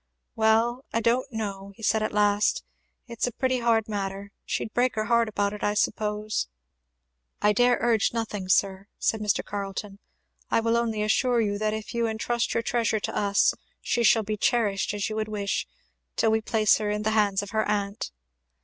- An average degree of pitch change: No, narrow, 2.1 semitones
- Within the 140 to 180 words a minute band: No, average, 200 wpm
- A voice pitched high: Yes, high, 215 Hz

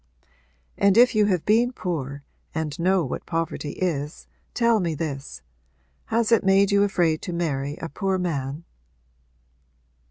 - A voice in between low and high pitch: Yes, medium, 175 Hz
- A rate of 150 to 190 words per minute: No, average, 140 wpm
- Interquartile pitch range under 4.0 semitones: No, average, 5.1 semitones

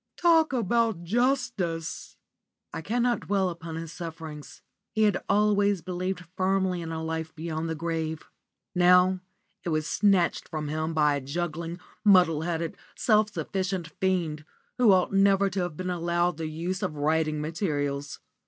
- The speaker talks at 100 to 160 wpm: Yes, average, 150 wpm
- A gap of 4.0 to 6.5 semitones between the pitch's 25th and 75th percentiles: No, average, 3.3 semitones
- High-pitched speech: No, medium, 175 Hz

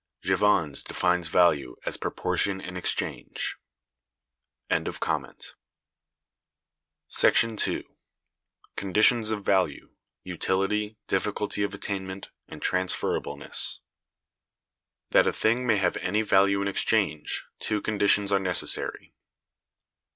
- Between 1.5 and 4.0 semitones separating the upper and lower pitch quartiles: Yes, narrow, 2.4 semitones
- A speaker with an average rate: No, slow, 90 wpm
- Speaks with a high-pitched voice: No, low, 100 Hz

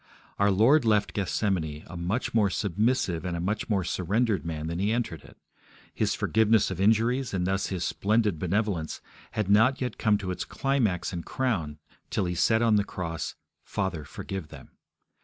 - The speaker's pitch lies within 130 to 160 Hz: No, low, 100 Hz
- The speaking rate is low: No, average, 175 wpm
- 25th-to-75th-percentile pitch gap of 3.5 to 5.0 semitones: Yes, average, 4.1 semitones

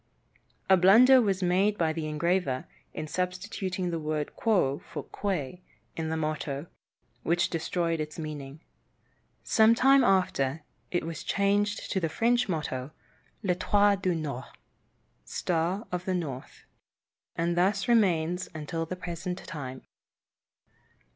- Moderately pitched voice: Yes, medium, 175 Hz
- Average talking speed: No, slow, 130 wpm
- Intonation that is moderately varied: Yes, average, 3.9 semitones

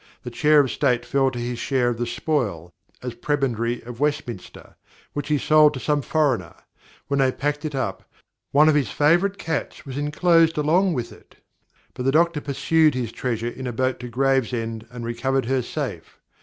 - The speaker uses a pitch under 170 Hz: Yes, low, 135 Hz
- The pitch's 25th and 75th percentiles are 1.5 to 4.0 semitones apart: Yes, average, 3.6 semitones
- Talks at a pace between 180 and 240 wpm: Yes, average, 185 wpm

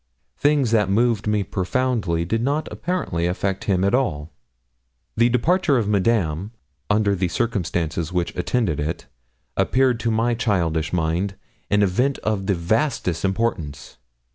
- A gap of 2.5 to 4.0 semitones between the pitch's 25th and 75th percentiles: No, average, 5.3 semitones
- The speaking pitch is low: Yes, low, 100 Hz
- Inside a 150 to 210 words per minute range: No, average, 140 wpm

